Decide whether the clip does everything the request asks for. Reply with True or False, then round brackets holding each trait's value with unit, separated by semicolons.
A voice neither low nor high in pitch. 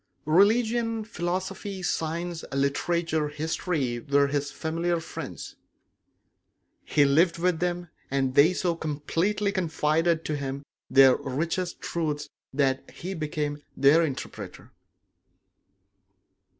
True (160 Hz)